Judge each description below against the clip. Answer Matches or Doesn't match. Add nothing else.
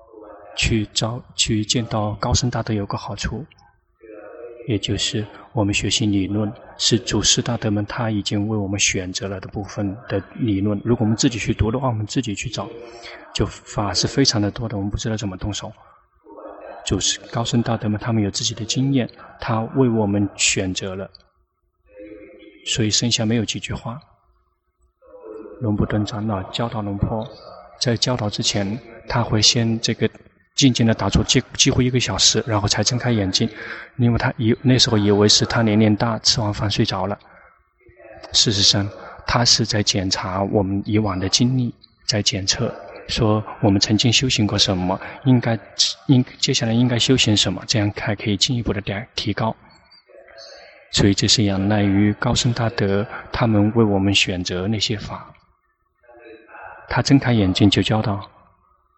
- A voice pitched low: Matches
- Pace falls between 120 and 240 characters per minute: Doesn't match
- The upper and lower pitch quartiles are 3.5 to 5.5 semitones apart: Doesn't match